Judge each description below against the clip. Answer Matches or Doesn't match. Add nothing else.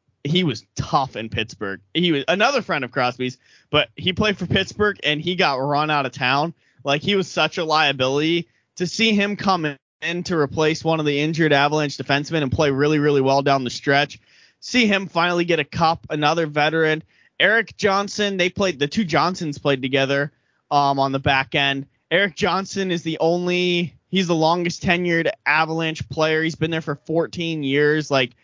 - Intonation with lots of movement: Doesn't match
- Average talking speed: Matches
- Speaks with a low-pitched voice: Doesn't match